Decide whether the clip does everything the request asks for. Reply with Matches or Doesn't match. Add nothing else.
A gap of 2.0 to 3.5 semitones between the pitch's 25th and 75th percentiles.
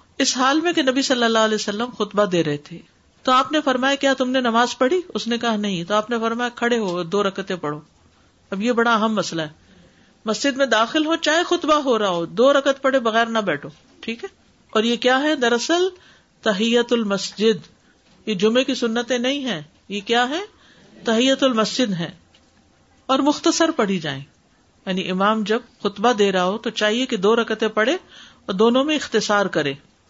Doesn't match